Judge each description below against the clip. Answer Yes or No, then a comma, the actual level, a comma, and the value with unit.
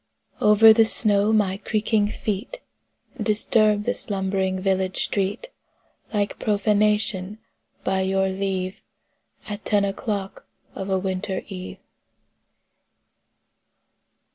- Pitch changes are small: Yes, narrow, 1.8 semitones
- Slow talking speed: Yes, slow, 95 wpm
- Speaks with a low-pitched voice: No, high, 200 Hz